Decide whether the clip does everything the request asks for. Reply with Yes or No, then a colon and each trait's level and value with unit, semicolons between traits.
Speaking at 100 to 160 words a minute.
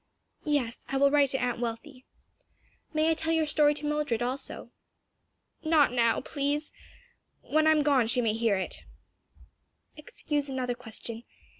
Yes: average, 150 wpm